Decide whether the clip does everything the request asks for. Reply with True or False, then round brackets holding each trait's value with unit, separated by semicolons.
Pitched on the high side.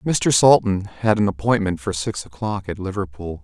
False (100 Hz)